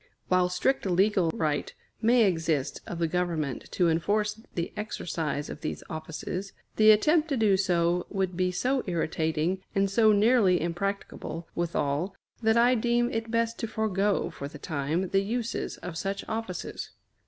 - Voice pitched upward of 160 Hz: Yes, medium, 185 Hz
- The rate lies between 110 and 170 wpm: Yes, average, 155 wpm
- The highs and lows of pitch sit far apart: No, average, 4.6 semitones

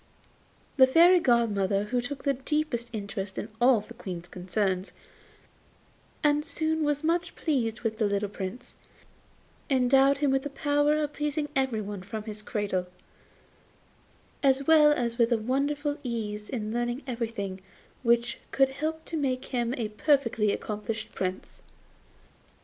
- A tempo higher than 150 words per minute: No, average, 140 wpm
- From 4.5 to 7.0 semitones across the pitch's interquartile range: Yes, average, 5.3 semitones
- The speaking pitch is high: Yes, high, 240 Hz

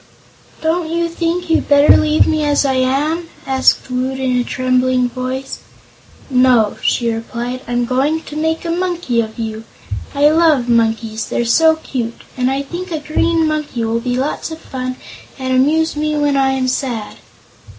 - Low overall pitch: No, very high, 265 Hz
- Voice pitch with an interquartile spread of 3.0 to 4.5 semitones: Yes, average, 4.1 semitones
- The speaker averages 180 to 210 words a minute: No, average, 170 wpm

